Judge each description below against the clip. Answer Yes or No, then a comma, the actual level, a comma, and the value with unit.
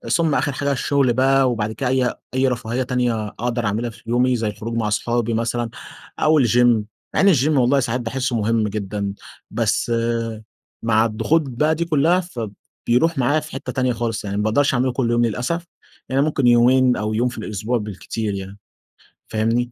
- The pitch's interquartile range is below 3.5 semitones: Yes, average, 3.0 semitones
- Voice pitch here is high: No, low, 120 Hz